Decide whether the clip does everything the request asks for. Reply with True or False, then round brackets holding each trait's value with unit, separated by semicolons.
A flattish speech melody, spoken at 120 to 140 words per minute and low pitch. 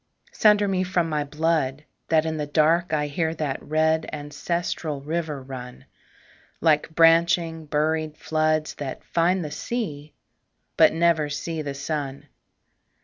False (2.0 semitones; 135 wpm; 155 Hz)